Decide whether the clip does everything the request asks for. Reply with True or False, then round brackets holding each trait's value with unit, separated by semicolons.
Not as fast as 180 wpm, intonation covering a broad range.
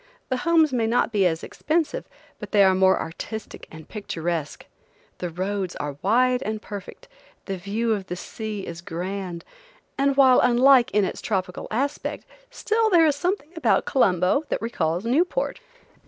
True (160 wpm; 6.5 semitones)